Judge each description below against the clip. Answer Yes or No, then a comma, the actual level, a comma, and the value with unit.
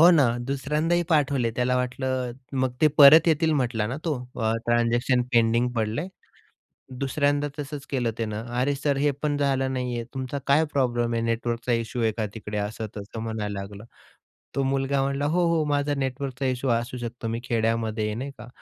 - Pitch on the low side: Yes, low, 125 Hz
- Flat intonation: No, average, 3.4 semitones